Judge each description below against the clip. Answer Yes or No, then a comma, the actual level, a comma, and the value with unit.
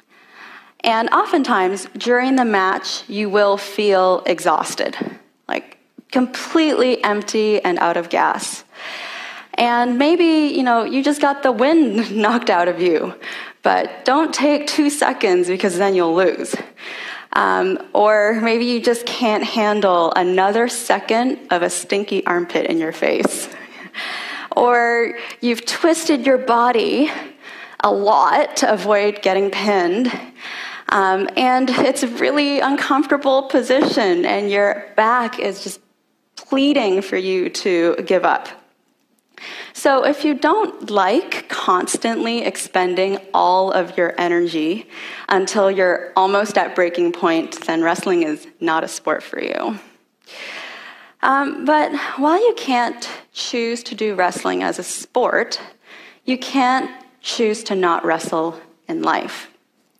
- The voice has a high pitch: Yes, high, 235 Hz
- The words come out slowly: Yes, slow, 130 wpm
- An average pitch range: No, wide, 6.5 semitones